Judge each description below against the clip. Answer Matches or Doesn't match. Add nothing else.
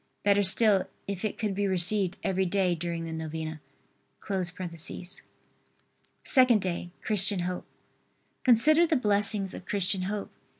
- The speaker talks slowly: Matches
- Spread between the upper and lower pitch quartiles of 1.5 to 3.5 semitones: Matches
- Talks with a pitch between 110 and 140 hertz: Doesn't match